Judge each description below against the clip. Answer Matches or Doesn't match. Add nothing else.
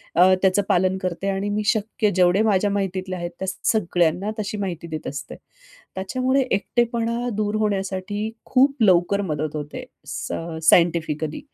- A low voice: Doesn't match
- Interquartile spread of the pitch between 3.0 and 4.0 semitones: Matches